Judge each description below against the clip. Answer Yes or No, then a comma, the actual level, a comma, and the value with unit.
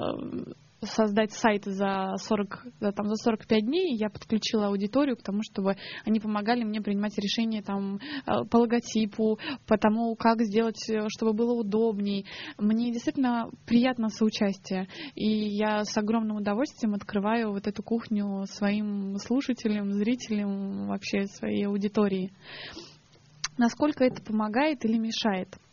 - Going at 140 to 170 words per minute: No, average, 125 wpm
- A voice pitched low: No, high, 215 Hz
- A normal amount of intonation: No, narrow, 2.1 semitones